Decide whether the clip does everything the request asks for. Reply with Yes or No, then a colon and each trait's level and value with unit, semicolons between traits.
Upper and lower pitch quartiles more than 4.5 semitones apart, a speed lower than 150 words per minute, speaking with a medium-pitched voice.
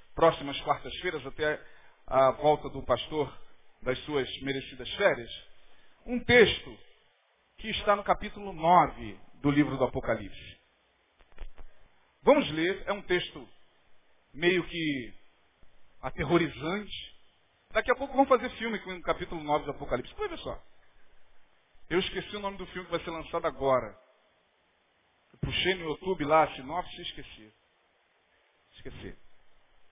Yes: wide, 5.6 semitones; average, 125 wpm; medium, 155 Hz